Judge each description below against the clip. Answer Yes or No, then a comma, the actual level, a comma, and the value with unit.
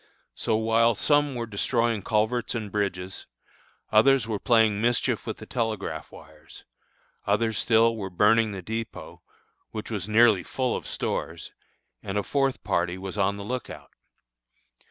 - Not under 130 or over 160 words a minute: Yes, average, 145 wpm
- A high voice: No, low, 110 Hz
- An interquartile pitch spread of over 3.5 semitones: No, narrow, 2.5 semitones